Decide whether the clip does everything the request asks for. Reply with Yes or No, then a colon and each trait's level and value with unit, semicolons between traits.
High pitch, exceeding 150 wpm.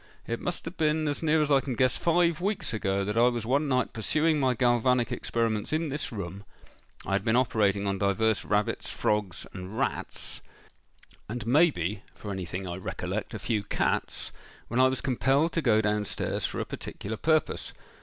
No: low, 115 Hz; average, 180 wpm